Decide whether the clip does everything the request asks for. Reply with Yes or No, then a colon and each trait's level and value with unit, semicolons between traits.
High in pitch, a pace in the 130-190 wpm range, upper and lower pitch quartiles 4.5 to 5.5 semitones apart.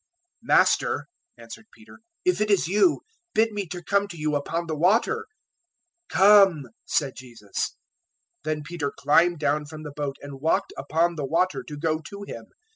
No: medium, 160 Hz; average, 170 wpm; average, 5.2 semitones